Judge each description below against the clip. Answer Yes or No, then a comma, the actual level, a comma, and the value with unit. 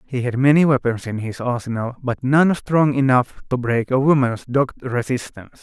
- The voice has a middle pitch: No, low, 130 Hz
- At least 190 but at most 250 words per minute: No, average, 180 wpm